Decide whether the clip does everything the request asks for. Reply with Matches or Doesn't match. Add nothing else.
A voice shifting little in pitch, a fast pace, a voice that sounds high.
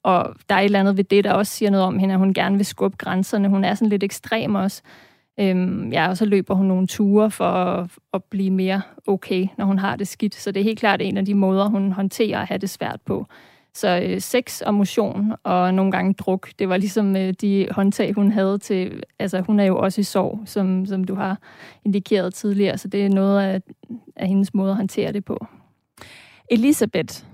Matches